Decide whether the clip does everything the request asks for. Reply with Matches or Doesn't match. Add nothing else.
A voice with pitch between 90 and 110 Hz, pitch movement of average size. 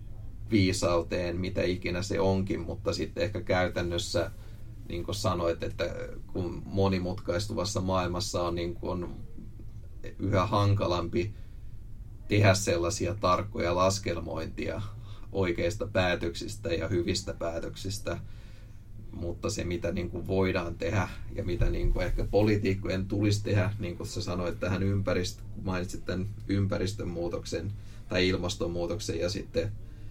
Matches